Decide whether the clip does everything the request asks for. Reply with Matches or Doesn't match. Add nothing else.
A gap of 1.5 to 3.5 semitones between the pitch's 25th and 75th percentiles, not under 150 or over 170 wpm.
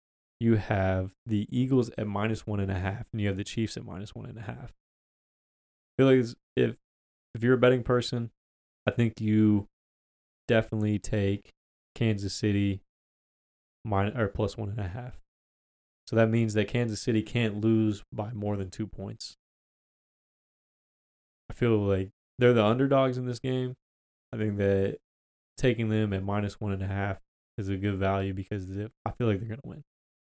Doesn't match